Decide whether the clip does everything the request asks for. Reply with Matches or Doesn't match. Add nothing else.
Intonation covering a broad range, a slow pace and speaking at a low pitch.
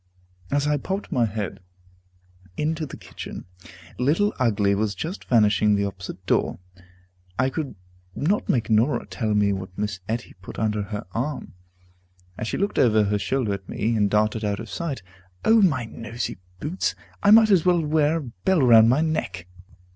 Doesn't match